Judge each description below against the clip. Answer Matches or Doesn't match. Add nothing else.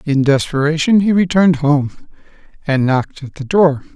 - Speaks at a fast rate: Doesn't match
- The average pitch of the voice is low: Doesn't match